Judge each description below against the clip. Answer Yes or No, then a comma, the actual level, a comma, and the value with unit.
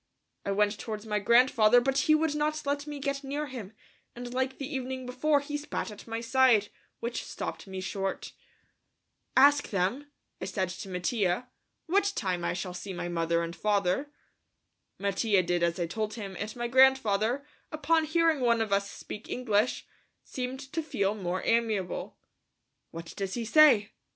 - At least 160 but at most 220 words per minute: Yes, average, 170 wpm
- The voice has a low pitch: No, high, 230 Hz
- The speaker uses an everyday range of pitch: No, wide, 5.7 semitones